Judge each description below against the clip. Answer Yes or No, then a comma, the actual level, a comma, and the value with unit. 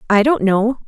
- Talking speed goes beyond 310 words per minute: No, fast, 205 wpm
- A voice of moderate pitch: No, high, 225 Hz